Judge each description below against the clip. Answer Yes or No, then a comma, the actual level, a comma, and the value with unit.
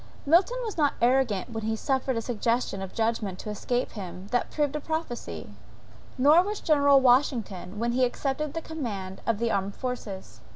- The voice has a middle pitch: No, high, 245 Hz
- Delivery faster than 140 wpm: Yes, average, 180 wpm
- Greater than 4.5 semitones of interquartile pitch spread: Yes, average, 5.2 semitones